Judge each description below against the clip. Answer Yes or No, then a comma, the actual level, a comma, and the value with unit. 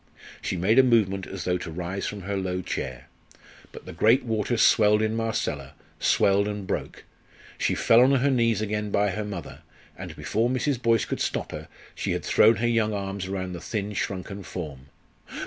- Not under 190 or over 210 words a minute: Yes, average, 195 wpm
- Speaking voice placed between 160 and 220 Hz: No, low, 105 Hz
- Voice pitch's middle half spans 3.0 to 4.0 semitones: Yes, average, 3.4 semitones